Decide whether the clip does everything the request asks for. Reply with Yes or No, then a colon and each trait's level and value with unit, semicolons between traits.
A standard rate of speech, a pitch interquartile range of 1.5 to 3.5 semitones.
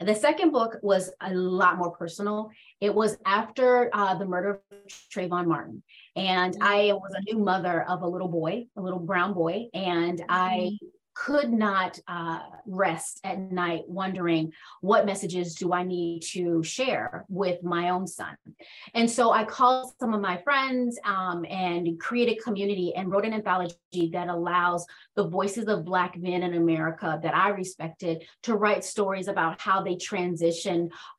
Yes: average, 165 wpm; average, 2.8 semitones